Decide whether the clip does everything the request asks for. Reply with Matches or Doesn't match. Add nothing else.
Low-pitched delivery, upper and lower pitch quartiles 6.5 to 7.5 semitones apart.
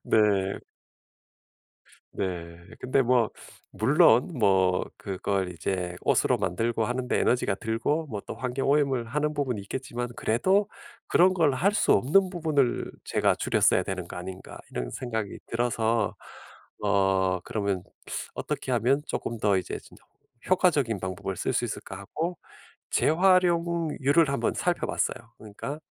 Matches